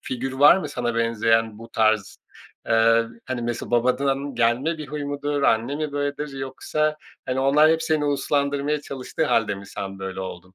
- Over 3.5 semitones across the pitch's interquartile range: Yes, average, 4.0 semitones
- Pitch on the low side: Yes, low, 130 Hz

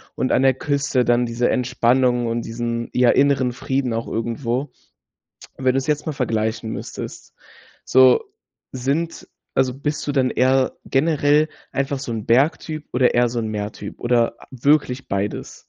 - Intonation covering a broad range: No, average, 2.7 semitones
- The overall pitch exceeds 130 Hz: No, low, 125 Hz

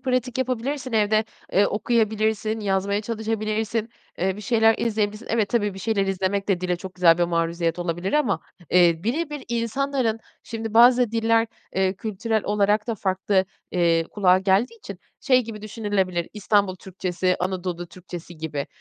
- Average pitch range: Yes, average, 3.5 semitones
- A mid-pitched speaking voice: No, high, 205 Hz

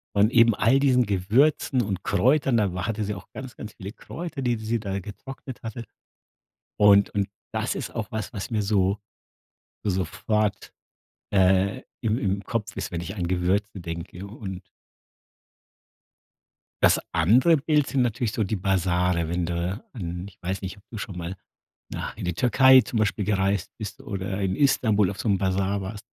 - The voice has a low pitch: Yes, low, 100 Hz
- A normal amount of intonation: Yes, average, 3.4 semitones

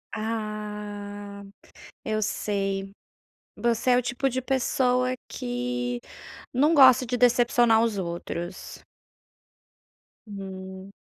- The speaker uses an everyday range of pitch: Yes, average, 4.0 semitones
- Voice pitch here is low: No, high, 215 Hz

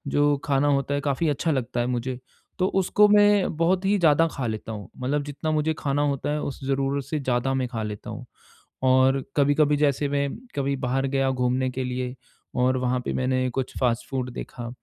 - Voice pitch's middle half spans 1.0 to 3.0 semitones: Yes, narrow, 2.4 semitones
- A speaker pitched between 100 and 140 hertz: Yes, low, 135 Hz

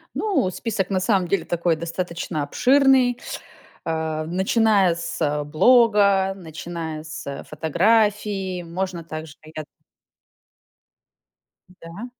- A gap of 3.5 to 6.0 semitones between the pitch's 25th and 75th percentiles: Yes, average, 4.5 semitones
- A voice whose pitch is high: No, medium, 180 Hz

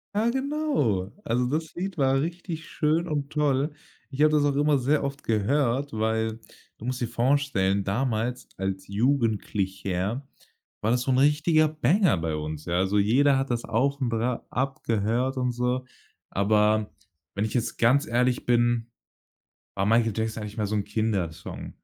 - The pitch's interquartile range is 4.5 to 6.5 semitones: Yes, average, 4.8 semitones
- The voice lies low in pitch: Yes, low, 125 Hz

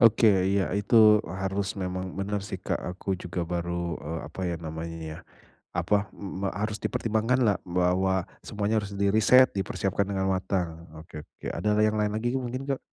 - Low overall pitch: Yes, low, 100 Hz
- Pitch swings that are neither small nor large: Yes, average, 3.0 semitones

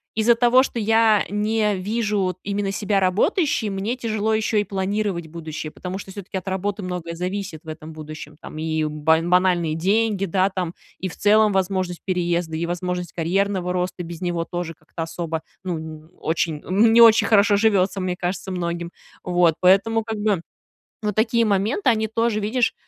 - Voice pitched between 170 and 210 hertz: Yes, high, 190 Hz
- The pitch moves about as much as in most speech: Yes, average, 3.6 semitones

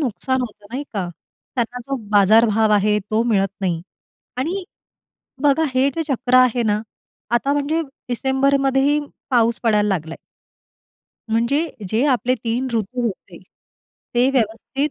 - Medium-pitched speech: No, high, 240 Hz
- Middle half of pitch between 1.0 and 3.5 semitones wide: No, average, 3.9 semitones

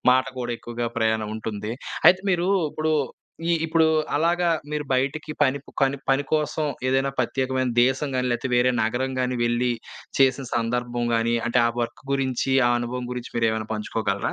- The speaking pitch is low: Yes, low, 125 Hz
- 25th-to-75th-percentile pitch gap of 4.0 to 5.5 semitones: No, average, 2.7 semitones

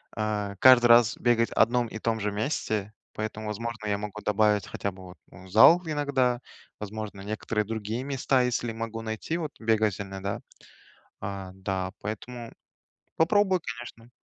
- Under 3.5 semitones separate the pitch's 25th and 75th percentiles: Yes, average, 2.8 semitones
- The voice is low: Yes, low, 110 Hz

